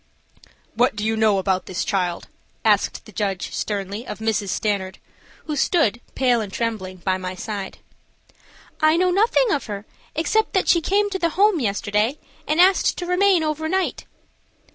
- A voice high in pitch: Yes, high, 225 Hz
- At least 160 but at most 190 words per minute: Yes, average, 165 wpm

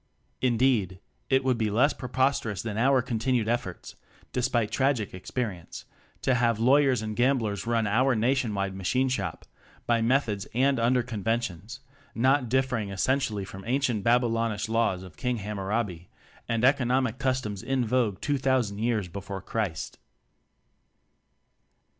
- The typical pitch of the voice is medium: No, low, 115 Hz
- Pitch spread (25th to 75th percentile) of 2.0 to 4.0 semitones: Yes, average, 3.7 semitones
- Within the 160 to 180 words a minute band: No, average, 140 wpm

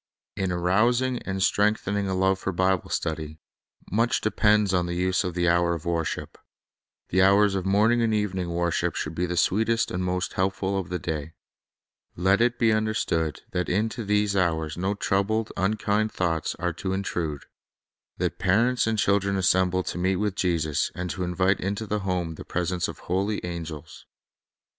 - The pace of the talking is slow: No, average, 180 wpm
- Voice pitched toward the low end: Yes, very low, 95 Hz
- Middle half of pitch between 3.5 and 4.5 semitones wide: No, average, 2.8 semitones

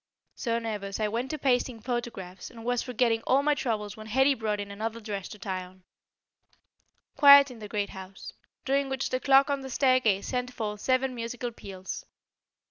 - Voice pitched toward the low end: No, high, 230 Hz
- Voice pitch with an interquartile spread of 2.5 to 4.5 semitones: Yes, average, 3.8 semitones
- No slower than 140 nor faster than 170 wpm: No, average, 185 wpm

